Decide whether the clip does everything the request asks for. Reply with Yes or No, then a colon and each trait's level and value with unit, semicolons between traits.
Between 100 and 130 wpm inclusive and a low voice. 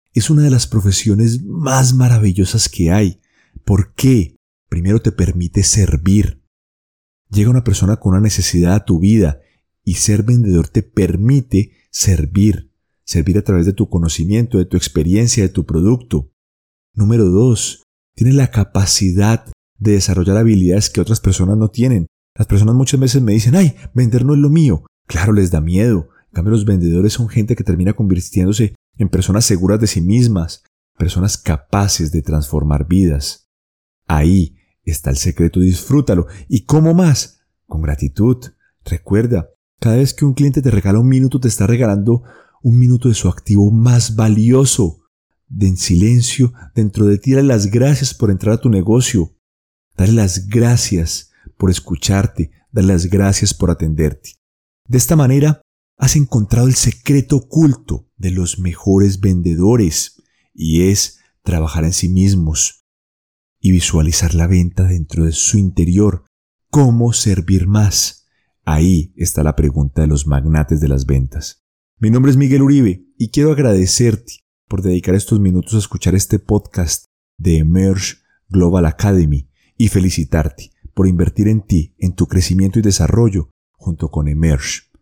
No: average, 155 wpm; very low, 95 Hz